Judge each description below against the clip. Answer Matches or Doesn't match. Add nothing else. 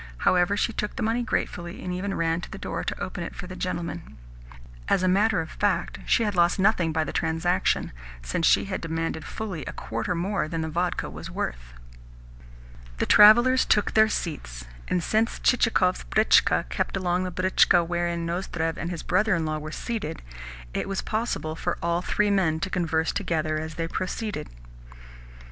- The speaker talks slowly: Doesn't match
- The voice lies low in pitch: Doesn't match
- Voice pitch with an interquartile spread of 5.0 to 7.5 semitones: Doesn't match